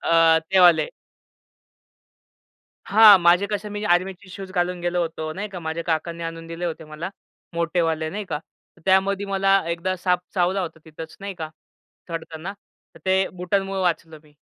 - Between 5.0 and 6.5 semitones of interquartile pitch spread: No, average, 2.7 semitones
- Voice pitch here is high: No, medium, 175 Hz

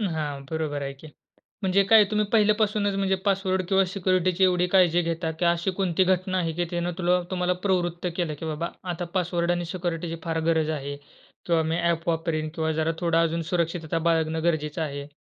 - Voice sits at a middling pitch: Yes, medium, 170 Hz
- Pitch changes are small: Yes, narrow, 2.3 semitones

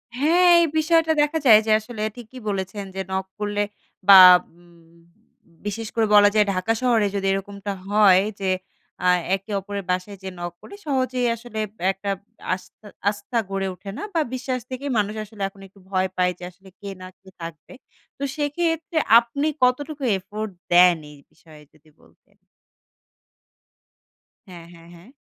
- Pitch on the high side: Yes, high, 205 Hz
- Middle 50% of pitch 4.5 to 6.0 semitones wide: Yes, average, 4.8 semitones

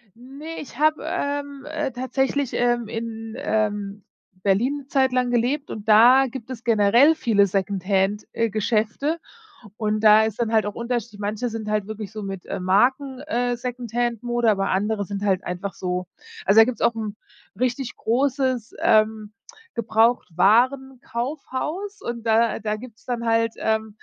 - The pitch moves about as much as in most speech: Yes, average, 3.3 semitones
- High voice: Yes, high, 230 Hz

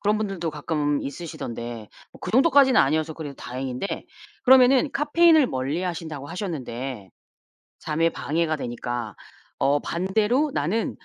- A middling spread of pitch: No, wide, 7.8 semitones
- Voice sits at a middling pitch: Yes, medium, 160 Hz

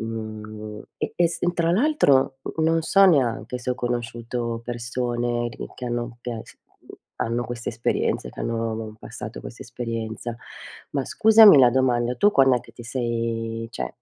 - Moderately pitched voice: No, low, 120 Hz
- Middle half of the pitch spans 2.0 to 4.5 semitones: Yes, narrow, 2.4 semitones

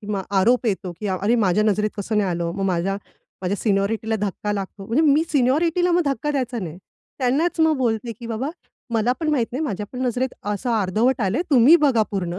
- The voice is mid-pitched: No, high, 225 Hz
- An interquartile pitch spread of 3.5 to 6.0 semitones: Yes, average, 4.7 semitones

